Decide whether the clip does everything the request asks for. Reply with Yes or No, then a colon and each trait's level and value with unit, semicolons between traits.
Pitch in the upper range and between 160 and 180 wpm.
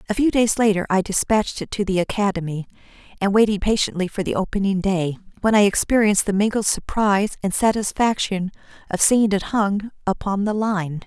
Yes: high, 200 Hz; average, 175 wpm